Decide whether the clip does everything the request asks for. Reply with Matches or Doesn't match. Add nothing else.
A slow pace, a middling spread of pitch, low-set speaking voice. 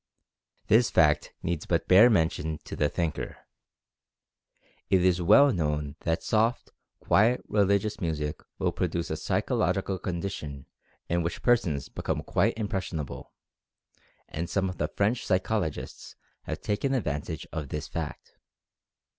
Matches